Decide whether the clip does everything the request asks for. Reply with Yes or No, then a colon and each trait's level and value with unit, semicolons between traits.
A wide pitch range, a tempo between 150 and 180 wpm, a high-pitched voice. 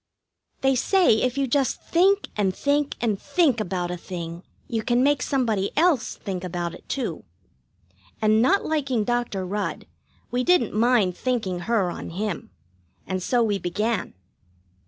Yes: wide, 6.0 semitones; average, 155 wpm; high, 225 Hz